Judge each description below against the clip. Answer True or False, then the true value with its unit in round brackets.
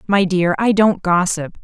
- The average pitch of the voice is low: False (185 Hz)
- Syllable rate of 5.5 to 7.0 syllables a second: False (4.2 syllables/s)